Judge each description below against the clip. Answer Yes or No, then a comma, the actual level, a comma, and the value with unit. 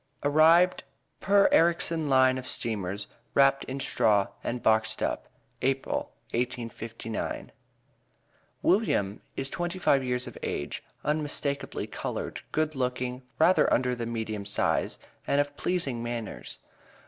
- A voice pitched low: Yes, low, 130 Hz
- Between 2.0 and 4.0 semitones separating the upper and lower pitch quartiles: No, average, 4.6 semitones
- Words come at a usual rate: No, slow, 120 wpm